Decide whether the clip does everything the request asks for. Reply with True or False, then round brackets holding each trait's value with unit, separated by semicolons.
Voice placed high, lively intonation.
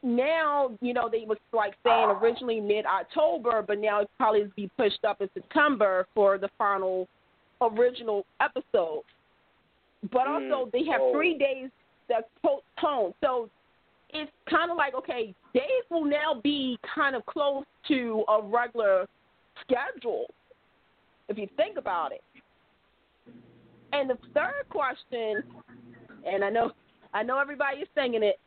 True (245 Hz; 5.7 semitones)